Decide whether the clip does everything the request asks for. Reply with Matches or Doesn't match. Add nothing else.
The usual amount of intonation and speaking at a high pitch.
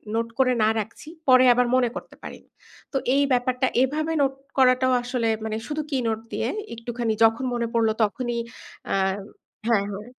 Doesn't match